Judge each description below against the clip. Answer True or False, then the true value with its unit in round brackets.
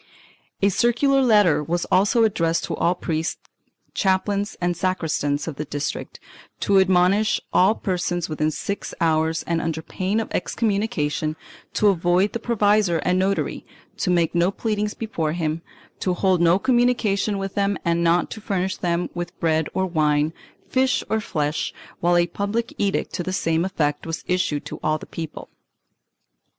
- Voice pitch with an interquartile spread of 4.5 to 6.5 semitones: False (3.6 semitones)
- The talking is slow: False (160 wpm)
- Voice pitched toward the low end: False (180 Hz)